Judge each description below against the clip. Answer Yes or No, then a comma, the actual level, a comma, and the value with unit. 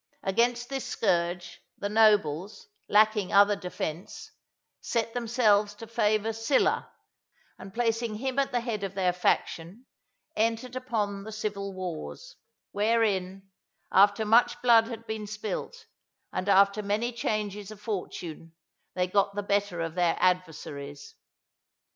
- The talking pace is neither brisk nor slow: No, slow, 130 wpm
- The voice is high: Yes, high, 205 Hz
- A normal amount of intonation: Yes, average, 3.3 semitones